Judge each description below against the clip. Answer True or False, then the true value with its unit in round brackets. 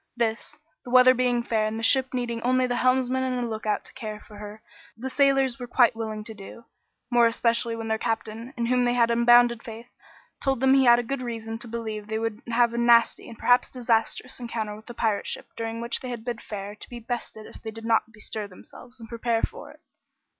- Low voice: False (235 Hz)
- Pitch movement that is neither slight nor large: False (1.7 semitones)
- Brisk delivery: True (225 wpm)